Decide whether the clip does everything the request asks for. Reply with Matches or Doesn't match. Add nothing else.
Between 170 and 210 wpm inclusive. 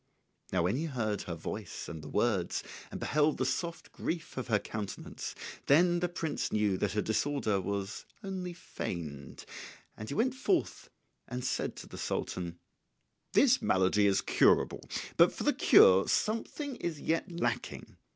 Doesn't match